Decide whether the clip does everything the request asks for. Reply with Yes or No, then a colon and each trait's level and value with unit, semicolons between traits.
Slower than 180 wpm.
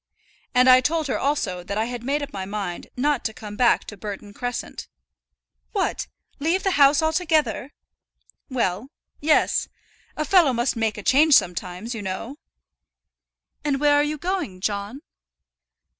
Yes: average, 155 wpm